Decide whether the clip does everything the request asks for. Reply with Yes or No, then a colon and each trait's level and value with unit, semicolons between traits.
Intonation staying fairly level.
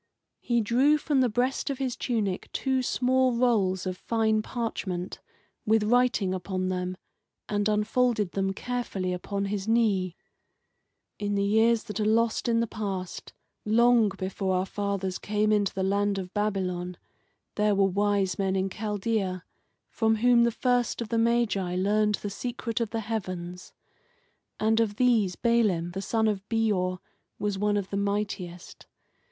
No: average, 3.3 semitones